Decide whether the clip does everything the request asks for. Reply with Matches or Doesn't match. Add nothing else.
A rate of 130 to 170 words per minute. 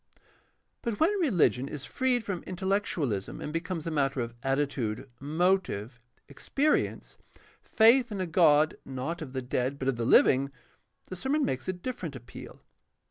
Matches